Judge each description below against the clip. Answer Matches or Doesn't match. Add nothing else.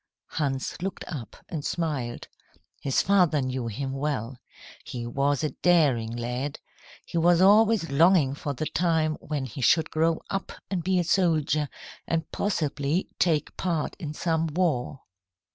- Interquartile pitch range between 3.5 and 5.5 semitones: Matches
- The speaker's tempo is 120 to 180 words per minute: Matches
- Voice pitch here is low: Doesn't match